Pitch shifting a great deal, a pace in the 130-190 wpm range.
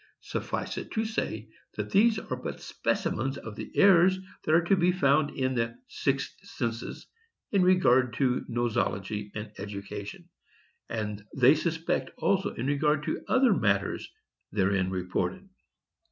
Yes: wide, 8.8 semitones; average, 140 wpm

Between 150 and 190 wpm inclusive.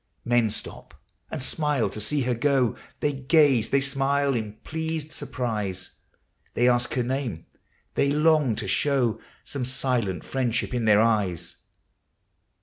No: average, 140 wpm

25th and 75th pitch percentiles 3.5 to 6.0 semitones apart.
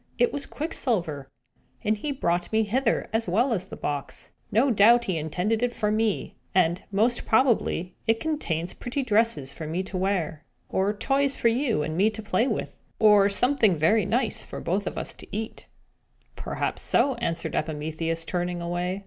Yes: average, 5.1 semitones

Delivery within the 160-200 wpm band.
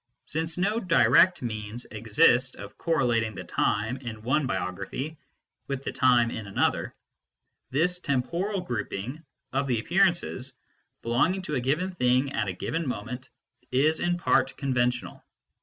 No: average, 140 wpm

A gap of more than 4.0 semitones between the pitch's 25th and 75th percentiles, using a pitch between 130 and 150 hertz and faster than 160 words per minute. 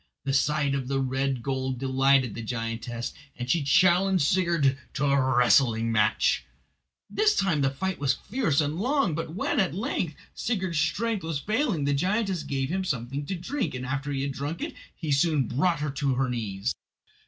Yes: average, 5.1 semitones; medium, 140 Hz; average, 185 wpm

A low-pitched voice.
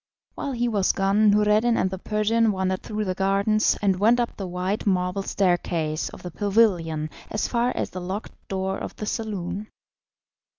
No: high, 200 Hz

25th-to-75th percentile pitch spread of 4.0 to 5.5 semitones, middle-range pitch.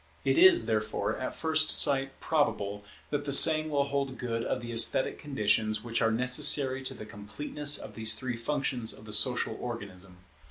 No: average, 4.6 semitones; low, 125 Hz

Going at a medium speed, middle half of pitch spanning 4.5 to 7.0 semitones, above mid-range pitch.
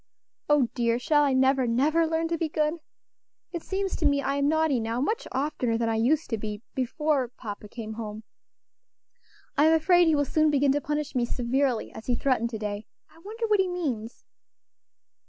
Yes: average, 190 wpm; average, 5.1 semitones; very high, 275 Hz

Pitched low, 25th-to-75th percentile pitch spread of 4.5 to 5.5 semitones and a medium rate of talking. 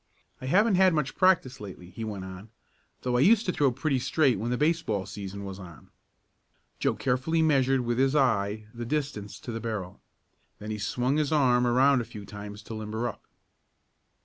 Yes: low, 125 Hz; average, 5.1 semitones; average, 190 wpm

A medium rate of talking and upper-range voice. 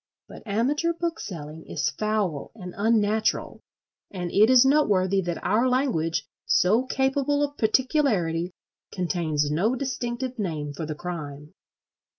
No: slow, 125 wpm; high, 205 Hz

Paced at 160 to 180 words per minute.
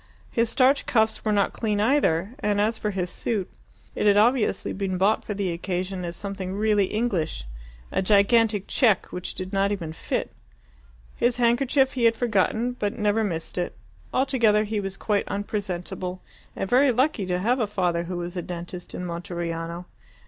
Yes: average, 175 wpm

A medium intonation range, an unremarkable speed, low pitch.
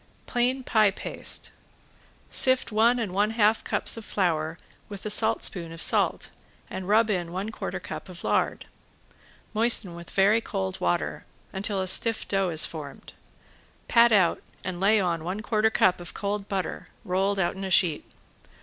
No: average, 3.6 semitones; average, 165 wpm; high, 195 Hz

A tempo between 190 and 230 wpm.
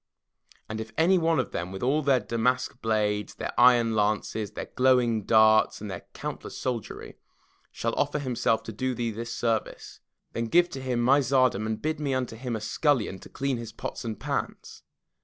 Yes: average, 195 wpm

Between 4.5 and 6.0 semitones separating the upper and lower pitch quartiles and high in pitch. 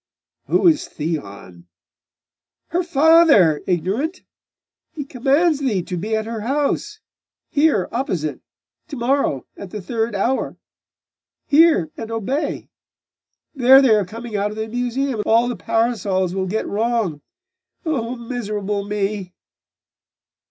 Yes: wide, 5.6 semitones; high, 225 Hz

